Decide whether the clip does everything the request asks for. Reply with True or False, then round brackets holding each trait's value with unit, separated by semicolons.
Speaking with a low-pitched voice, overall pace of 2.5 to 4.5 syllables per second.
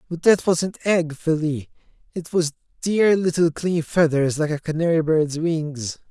False (160 Hz; 4.2 syllables/s)